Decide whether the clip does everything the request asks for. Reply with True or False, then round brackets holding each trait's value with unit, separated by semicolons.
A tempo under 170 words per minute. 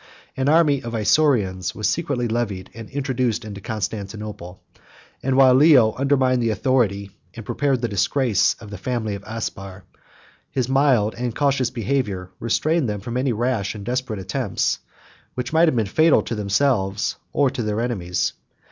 True (160 wpm)